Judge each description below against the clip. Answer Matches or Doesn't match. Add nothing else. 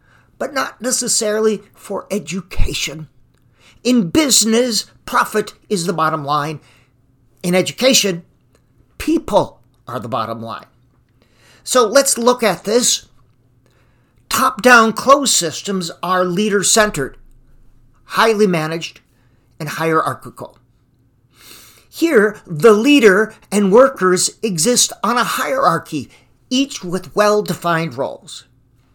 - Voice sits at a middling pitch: Matches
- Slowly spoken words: Matches